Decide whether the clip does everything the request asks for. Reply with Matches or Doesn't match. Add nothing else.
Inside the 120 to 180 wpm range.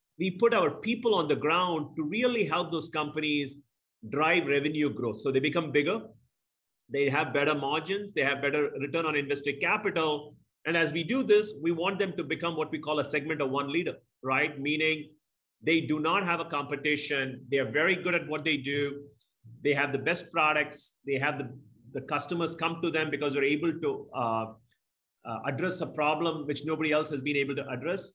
Doesn't match